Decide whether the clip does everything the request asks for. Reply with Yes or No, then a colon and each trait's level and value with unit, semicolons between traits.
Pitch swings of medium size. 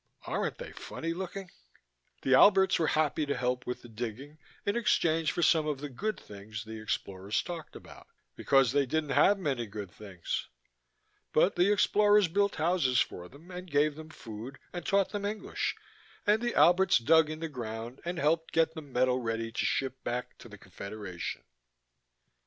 No: wide, 6.9 semitones